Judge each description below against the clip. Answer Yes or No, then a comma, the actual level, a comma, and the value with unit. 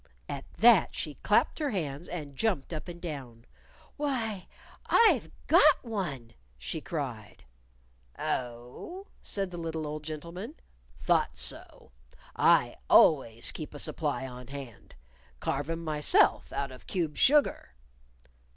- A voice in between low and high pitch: Yes, medium, 155 Hz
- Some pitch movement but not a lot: No, wide, 6.3 semitones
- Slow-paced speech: Yes, slow, 125 wpm